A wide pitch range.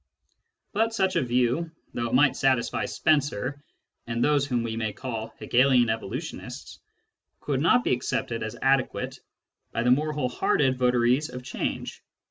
No: average, 3.2 semitones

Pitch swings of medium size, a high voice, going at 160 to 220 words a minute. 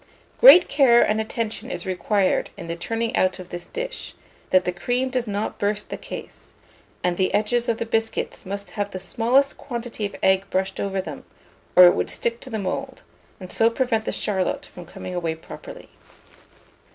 Yes: average, 3.9 semitones; high, 205 Hz; average, 190 wpm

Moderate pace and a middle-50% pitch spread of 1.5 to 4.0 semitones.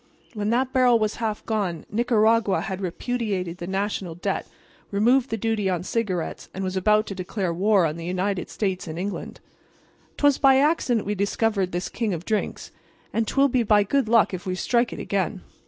Yes: average, 190 wpm; average, 3.7 semitones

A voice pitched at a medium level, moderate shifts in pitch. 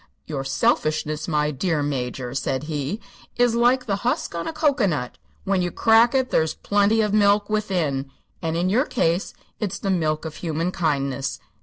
No: medium, 170 Hz; wide, 5.9 semitones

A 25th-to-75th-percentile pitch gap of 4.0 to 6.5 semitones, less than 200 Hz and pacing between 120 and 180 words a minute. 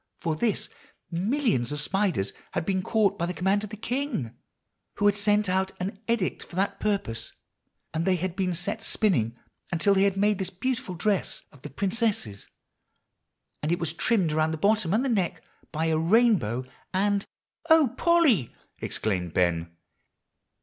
Yes: average, 4.8 semitones; high, 190 Hz; average, 165 wpm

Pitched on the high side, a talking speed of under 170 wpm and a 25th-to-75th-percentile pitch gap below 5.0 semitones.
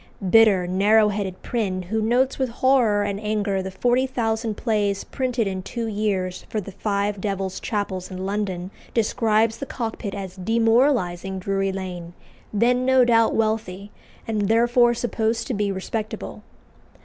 Yes: high, 210 Hz; average, 150 wpm; average, 3.0 semitones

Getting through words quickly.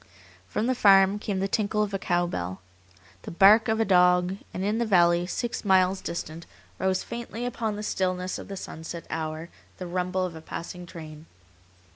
No: average, 185 wpm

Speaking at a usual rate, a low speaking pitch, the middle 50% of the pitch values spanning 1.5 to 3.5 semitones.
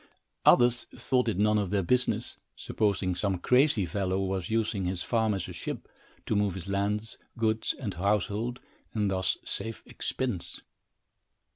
Yes: average, 150 wpm; low, 105 Hz; average, 2.8 semitones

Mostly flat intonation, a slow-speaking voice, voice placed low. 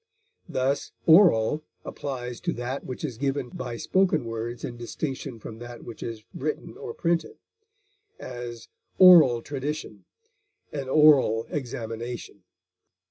No: average, 3.9 semitones; slow, 120 wpm; low, 125 Hz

